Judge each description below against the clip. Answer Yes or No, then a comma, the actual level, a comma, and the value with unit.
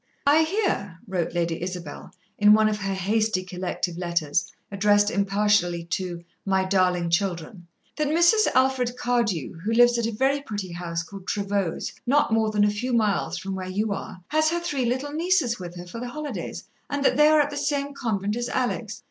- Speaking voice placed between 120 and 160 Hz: No, high, 210 Hz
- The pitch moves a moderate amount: No, wide, 5.9 semitones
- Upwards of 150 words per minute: Yes, average, 190 wpm